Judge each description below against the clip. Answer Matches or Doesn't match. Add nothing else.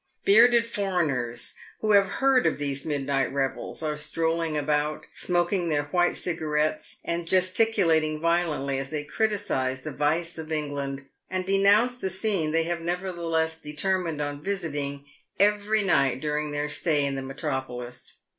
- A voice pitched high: Doesn't match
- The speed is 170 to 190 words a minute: Doesn't match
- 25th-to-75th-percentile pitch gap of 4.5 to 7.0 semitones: Doesn't match